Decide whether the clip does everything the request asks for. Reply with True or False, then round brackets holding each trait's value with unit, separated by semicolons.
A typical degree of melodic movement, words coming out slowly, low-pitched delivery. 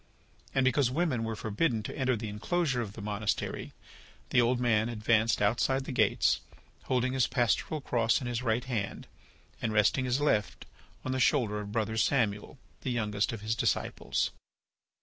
False (3.2 semitones; 170 wpm; 115 Hz)